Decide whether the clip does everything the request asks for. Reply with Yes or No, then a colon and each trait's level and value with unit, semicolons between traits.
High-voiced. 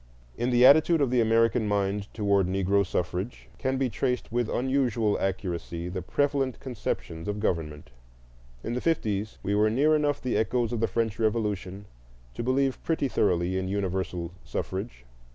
No: low, 110 Hz